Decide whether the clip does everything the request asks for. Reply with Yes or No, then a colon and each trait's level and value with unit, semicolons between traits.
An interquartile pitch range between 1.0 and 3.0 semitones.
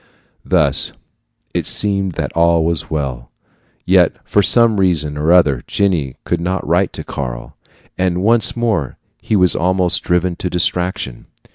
No: average, 3.6 semitones